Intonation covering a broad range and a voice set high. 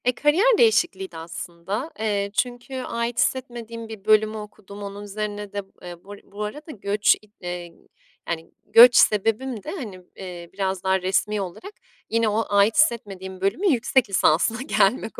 No: average, 3.8 semitones; high, 210 Hz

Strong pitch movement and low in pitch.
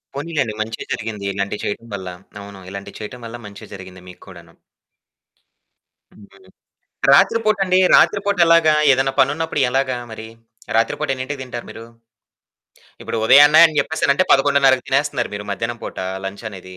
Yes: wide, 6.1 semitones; low, 120 Hz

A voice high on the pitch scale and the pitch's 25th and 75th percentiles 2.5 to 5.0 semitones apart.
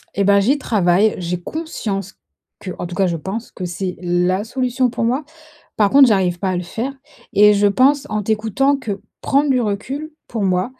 No: high, 205 Hz; wide, 5.4 semitones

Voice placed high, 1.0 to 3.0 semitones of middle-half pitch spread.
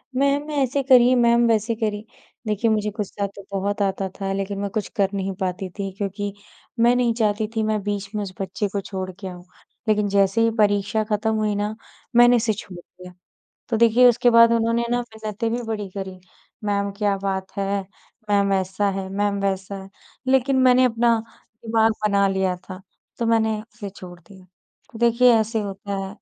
Yes: high, 210 Hz; average, 2.7 semitones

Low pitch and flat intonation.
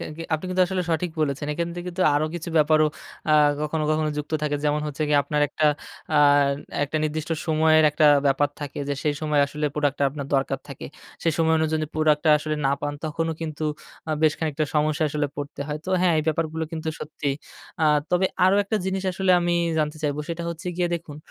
No: medium, 155 Hz; narrow, 1.7 semitones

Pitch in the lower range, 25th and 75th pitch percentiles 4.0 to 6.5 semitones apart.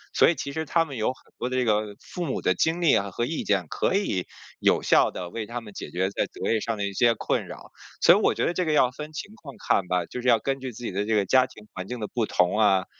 Yes: low, 115 Hz; wide, 5.4 semitones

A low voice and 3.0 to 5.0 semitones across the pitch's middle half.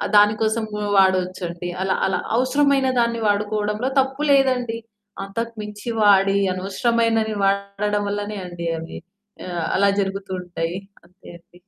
No: high, 205 Hz; average, 3.3 semitones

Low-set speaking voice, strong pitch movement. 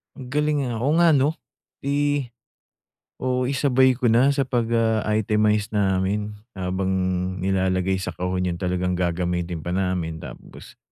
Yes: low, 105 Hz; wide, 6.1 semitones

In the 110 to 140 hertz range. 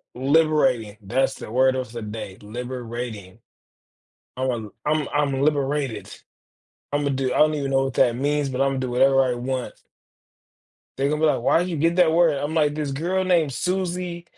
Yes: low, 135 Hz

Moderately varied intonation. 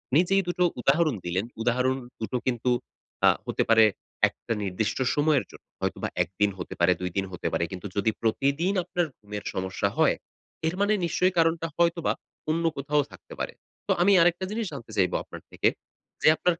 No: wide, 8.5 semitones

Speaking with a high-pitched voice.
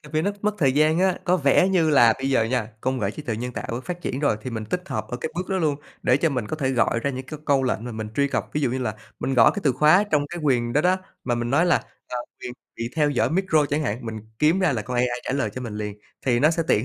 No: low, 135 Hz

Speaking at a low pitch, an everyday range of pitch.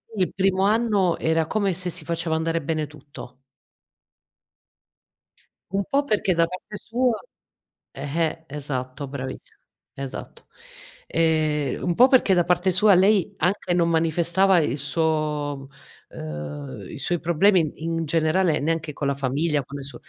No: medium, 165 Hz; average, 4.1 semitones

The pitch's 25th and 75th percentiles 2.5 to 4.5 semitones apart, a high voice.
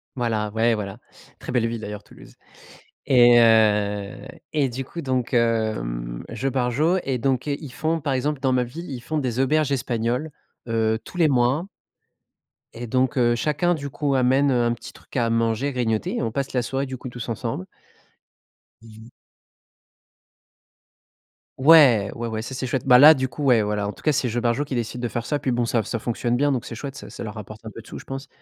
No: average, 3.1 semitones; low, 125 Hz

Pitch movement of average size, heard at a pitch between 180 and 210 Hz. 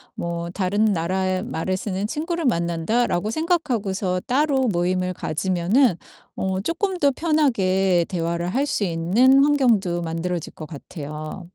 No: wide, 6.9 semitones; high, 190 Hz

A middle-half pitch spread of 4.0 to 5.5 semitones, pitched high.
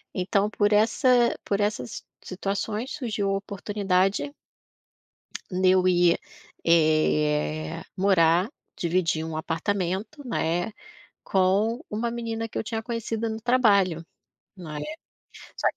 Yes: average, 4.4 semitones; high, 195 Hz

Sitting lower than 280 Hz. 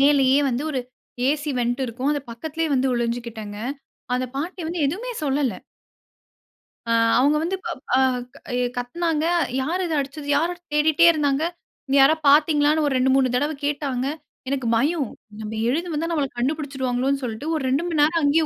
No: very high, 285 Hz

